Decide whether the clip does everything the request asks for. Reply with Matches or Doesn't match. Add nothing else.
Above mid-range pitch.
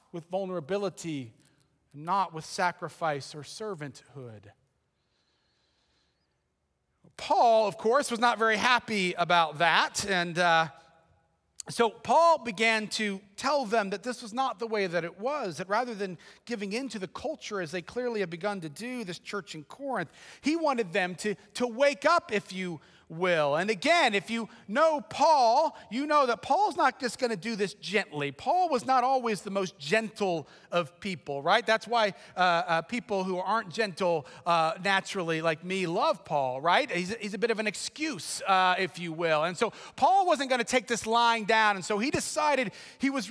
Matches